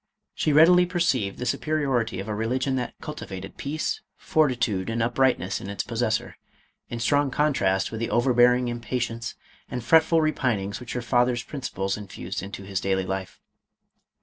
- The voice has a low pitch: Yes, low, 120 Hz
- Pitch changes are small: No, average, 5.3 semitones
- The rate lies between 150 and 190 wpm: Yes, average, 165 wpm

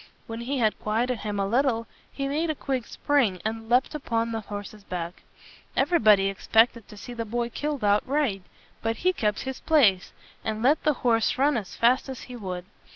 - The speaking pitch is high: Yes, high, 230 Hz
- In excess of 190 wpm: Yes, average, 200 wpm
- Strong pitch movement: No, average, 4.1 semitones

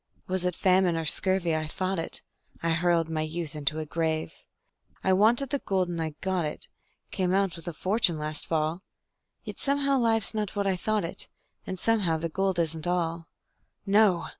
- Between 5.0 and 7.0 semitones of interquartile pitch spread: No, average, 3.1 semitones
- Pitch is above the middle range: No, medium, 175 Hz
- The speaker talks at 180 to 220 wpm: Yes, average, 190 wpm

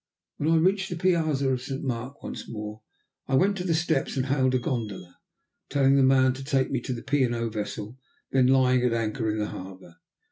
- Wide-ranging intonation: No, average, 3.3 semitones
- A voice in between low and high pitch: No, low, 130 Hz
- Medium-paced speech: No, fast, 220 wpm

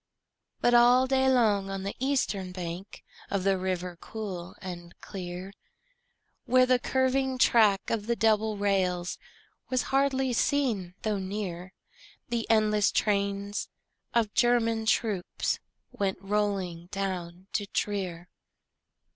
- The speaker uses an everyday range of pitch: Yes, average, 4.0 semitones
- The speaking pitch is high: Yes, high, 205 Hz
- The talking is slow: Yes, slow, 120 wpm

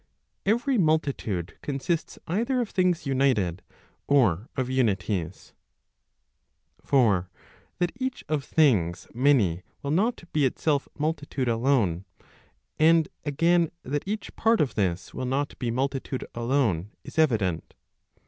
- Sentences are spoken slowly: Yes, slow, 120 wpm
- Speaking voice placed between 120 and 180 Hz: Yes, low, 135 Hz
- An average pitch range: No, wide, 6.8 semitones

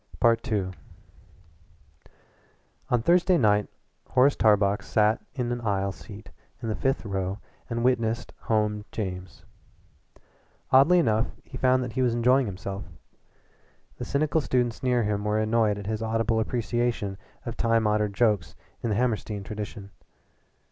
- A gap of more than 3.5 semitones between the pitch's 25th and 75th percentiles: No, average, 2.9 semitones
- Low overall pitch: Yes, low, 110 Hz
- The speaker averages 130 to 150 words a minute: Yes, slow, 135 wpm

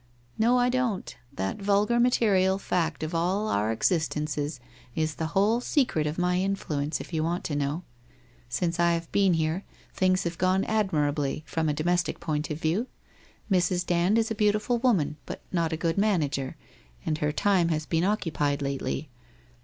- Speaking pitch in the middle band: Yes, medium, 170 Hz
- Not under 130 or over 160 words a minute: No, average, 175 wpm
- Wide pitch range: No, average, 4.3 semitones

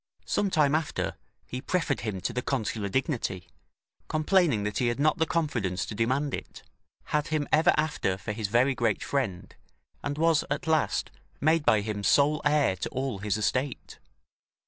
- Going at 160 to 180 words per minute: Yes, average, 170 wpm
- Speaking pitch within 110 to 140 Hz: Yes, low, 135 Hz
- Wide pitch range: Yes, wide, 6.2 semitones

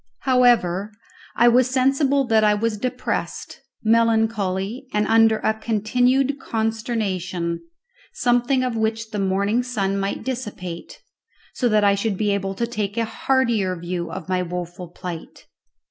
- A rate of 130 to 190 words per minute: Yes, average, 140 wpm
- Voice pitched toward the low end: No, high, 220 Hz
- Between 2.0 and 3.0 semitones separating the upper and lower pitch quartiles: No, average, 3.8 semitones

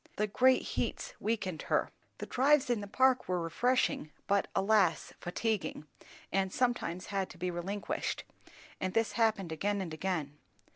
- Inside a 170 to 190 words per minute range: No, average, 150 wpm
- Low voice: No, high, 200 Hz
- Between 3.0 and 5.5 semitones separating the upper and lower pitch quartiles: Yes, average, 4.3 semitones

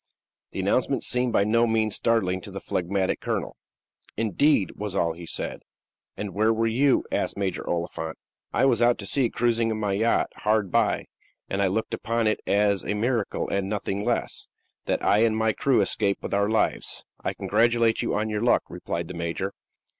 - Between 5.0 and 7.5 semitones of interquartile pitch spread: No, average, 2.8 semitones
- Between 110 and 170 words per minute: No, average, 190 wpm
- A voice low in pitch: Yes, low, 105 Hz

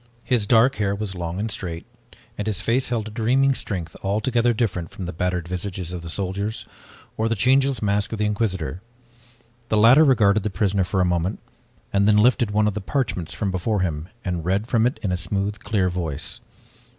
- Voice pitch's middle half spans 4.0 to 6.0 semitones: No, average, 3.6 semitones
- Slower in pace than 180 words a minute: No, average, 200 wpm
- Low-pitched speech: Yes, low, 100 Hz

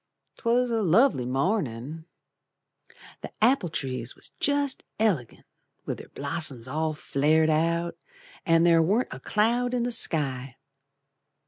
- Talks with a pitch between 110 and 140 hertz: No, medium, 165 Hz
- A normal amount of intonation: No, wide, 8.2 semitones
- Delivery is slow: Yes, slow, 125 wpm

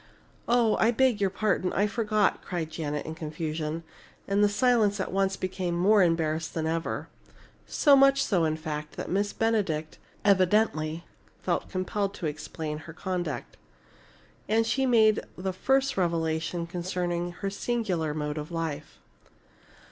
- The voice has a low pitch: No, medium, 180 Hz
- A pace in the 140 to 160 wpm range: Yes, average, 145 wpm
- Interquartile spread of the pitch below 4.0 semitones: No, average, 4.8 semitones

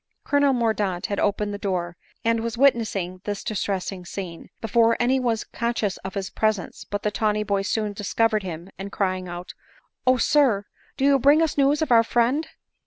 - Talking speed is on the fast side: Yes, fast, 210 wpm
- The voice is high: Yes, high, 215 Hz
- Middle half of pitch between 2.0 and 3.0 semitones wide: No, average, 3.6 semitones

